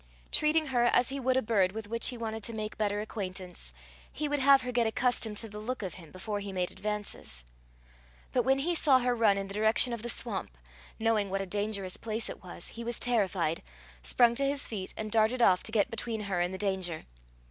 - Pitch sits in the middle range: No, high, 220 Hz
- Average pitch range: Yes, average, 3.6 semitones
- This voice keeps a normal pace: No, fast, 225 wpm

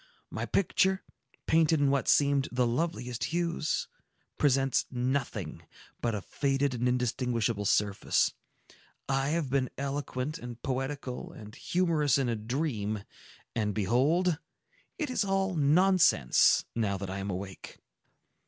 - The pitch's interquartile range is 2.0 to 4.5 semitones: No, average, 4.9 semitones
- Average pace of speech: No, slow, 125 wpm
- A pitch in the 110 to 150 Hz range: Yes, low, 135 Hz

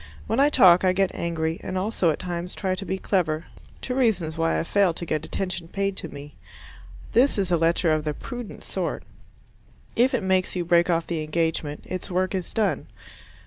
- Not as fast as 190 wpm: No, average, 200 wpm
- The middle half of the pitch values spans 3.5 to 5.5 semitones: No, average, 3.1 semitones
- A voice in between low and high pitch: Yes, medium, 180 Hz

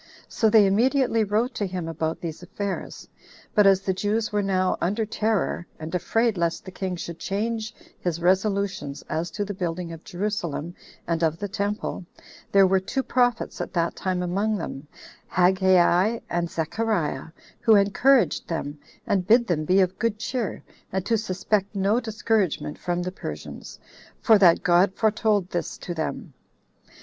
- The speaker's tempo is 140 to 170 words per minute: Yes, average, 160 wpm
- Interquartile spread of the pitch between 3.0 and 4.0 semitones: Yes, average, 3.6 semitones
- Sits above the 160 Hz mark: Yes, high, 190 Hz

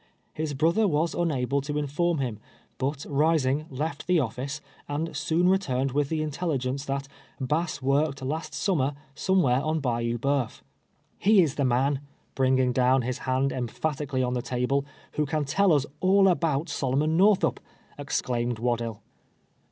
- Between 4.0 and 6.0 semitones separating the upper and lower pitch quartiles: No, average, 3.5 semitones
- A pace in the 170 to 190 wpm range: No, average, 160 wpm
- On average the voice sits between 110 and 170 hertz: Yes, medium, 140 Hz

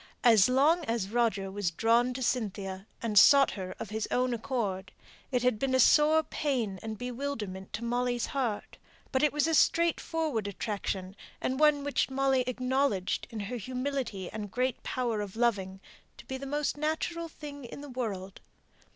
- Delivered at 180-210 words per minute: No, average, 170 wpm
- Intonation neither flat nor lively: Yes, average, 5.0 semitones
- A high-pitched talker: Yes, high, 245 Hz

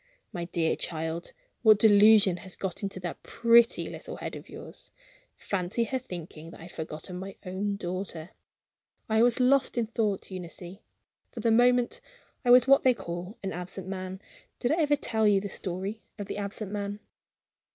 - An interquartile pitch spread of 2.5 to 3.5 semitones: No, average, 4.1 semitones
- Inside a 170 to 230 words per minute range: Yes, average, 175 wpm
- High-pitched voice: Yes, high, 200 Hz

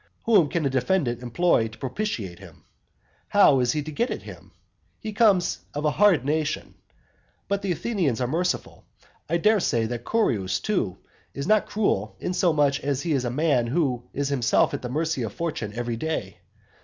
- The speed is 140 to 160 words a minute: No, average, 180 wpm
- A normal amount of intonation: No, wide, 6.7 semitones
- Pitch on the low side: No, medium, 145 Hz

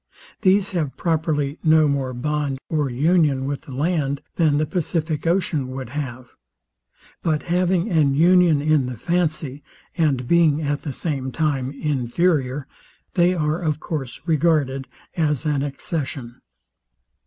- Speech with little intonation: No, average, 3.4 semitones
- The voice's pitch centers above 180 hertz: No, medium, 150 Hz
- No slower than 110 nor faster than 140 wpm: Yes, slow, 135 wpm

